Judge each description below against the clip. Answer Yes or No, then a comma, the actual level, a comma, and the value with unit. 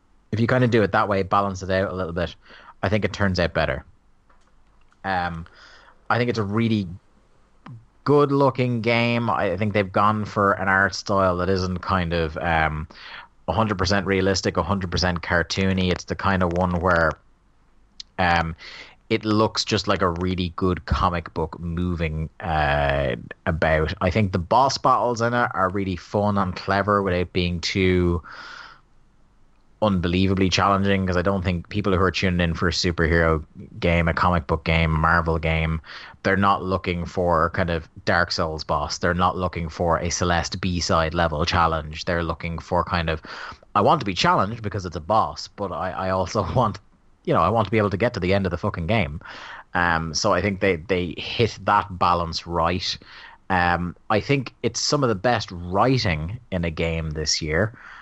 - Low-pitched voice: Yes, very low, 95 Hz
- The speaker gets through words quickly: No, average, 185 wpm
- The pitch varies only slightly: No, average, 3.0 semitones